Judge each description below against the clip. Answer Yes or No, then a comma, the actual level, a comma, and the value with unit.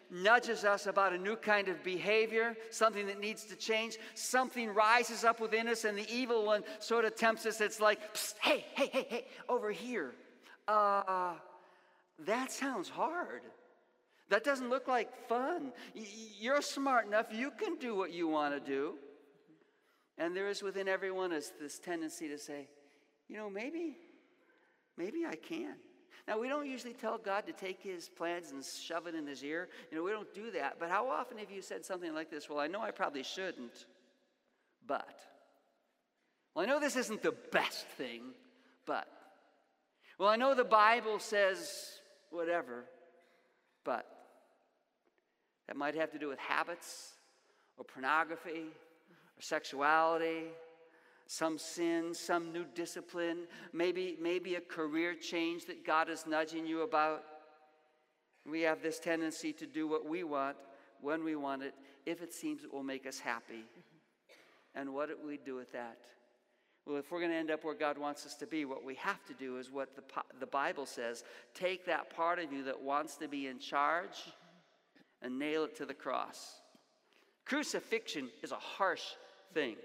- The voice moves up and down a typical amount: No, wide, 6.3 semitones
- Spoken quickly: No, average, 170 wpm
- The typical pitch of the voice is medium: Yes, medium, 175 Hz